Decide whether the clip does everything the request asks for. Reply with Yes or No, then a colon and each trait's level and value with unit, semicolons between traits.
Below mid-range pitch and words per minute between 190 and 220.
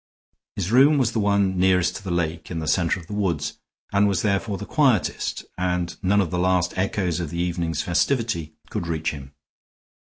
Yes: very low, 90 Hz; average, 195 wpm